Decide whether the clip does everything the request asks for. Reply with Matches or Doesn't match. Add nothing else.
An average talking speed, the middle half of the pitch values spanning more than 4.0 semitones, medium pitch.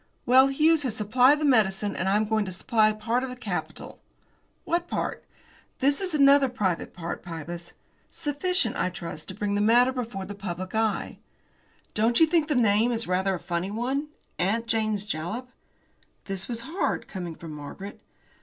Doesn't match